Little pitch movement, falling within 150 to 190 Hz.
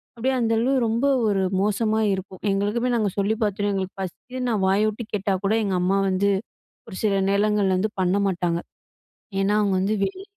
No: narrow, 2.3 semitones; high, 205 Hz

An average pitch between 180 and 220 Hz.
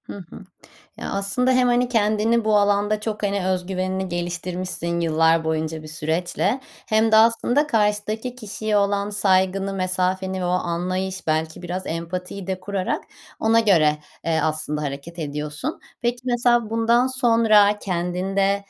Yes: high, 190 Hz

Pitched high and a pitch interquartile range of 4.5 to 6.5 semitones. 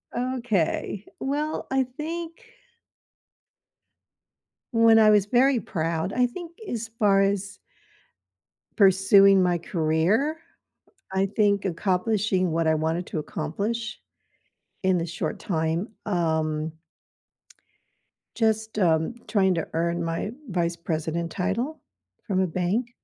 Yes: high, 195 Hz; average, 5.1 semitones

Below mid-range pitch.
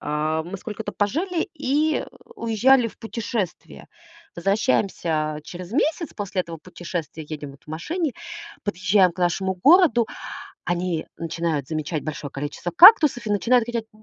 No: high, 190 Hz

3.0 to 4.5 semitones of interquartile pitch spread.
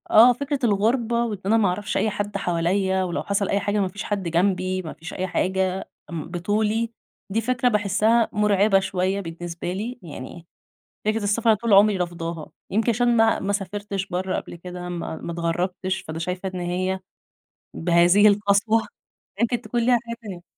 Yes: average, 3.3 semitones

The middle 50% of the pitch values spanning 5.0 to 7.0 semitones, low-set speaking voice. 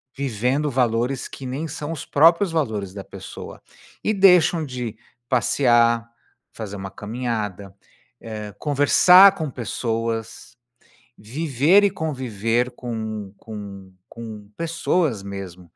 Yes: wide, 5.6 semitones; low, 120 Hz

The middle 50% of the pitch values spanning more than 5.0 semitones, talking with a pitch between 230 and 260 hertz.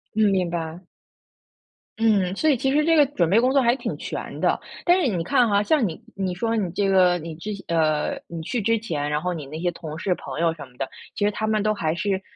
No: wide, 5.4 semitones; high, 195 Hz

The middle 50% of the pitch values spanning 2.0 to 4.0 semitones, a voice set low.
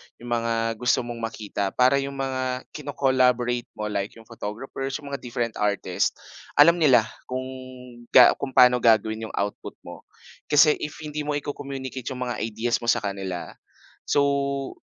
Yes: average, 3.4 semitones; low, 125 Hz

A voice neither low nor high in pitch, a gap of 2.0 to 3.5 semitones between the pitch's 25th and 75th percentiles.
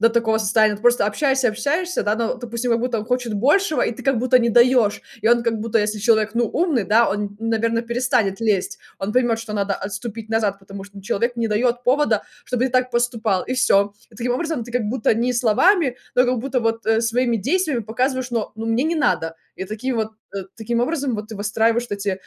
No: high, 230 Hz; average, 2.7 semitones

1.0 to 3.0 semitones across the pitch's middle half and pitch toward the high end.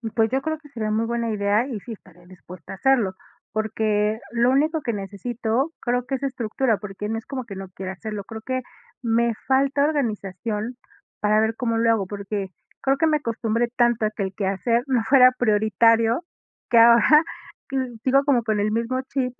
No: average, 3.4 semitones; high, 230 Hz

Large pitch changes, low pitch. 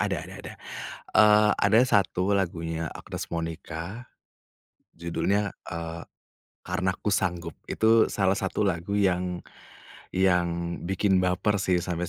No: average, 2.9 semitones; very low, 90 Hz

